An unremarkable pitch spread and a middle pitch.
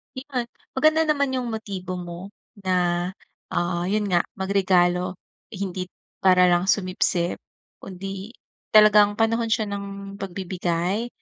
No: average, 3.0 semitones; high, 195 Hz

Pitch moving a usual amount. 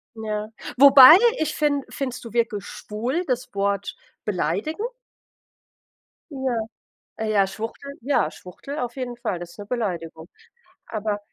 Yes: average, 4.7 semitones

